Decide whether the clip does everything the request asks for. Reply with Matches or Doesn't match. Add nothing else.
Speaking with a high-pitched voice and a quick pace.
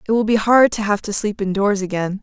Matches